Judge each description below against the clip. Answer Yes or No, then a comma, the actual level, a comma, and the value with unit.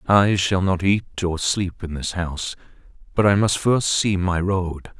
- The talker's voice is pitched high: No, very low, 95 Hz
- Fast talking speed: No, average, 190 wpm